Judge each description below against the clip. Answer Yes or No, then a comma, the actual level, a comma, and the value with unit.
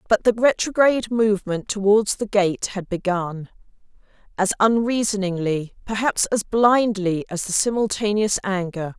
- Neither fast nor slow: No, slow, 115 wpm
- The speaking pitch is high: Yes, high, 205 Hz